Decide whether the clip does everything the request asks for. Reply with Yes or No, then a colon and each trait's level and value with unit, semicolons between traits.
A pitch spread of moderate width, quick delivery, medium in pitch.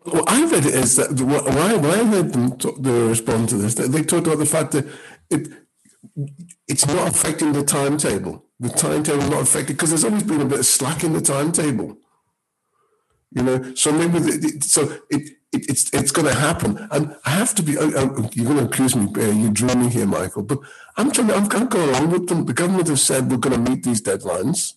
Yes: average, 5.0 semitones; fast, 220 wpm; medium, 150 Hz